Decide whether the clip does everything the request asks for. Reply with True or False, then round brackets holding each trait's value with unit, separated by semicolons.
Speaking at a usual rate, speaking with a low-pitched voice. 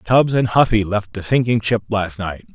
False (210 wpm; 110 Hz)